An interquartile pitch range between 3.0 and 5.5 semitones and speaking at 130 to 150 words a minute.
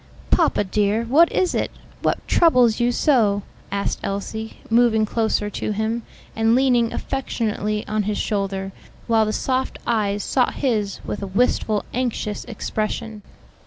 No: narrow, 2.6 semitones; average, 140 wpm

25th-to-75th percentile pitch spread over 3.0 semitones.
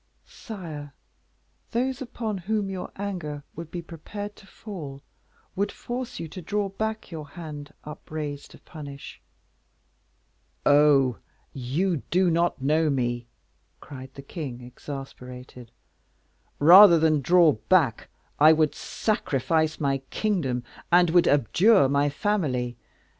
Yes: average, 5.2 semitones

